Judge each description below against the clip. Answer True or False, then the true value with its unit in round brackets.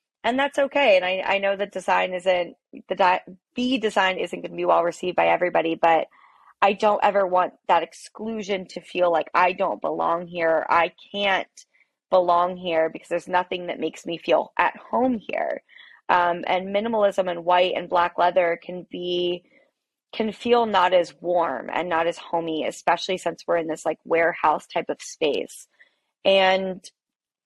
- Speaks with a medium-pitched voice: True (180 Hz)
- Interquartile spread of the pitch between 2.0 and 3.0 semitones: True (2.7 semitones)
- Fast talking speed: False (175 wpm)